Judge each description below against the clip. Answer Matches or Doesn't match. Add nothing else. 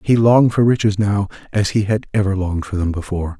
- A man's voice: Matches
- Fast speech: Matches